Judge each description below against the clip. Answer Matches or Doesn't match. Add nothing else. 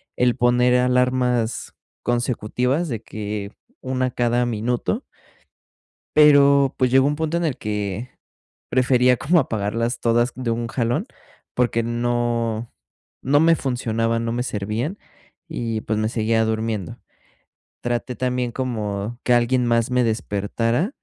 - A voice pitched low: Matches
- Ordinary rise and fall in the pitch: Doesn't match